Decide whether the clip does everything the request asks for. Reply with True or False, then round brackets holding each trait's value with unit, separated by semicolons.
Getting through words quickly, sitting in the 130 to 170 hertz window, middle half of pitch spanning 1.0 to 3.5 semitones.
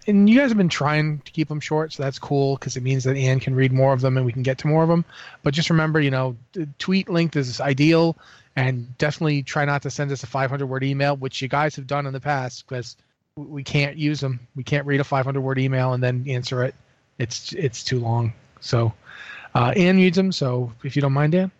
True (255 wpm; 140 Hz; 2.4 semitones)